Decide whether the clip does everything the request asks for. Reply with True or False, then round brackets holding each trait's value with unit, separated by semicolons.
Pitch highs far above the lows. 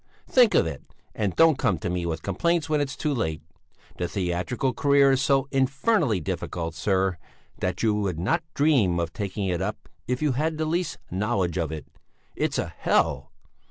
True (8.2 semitones)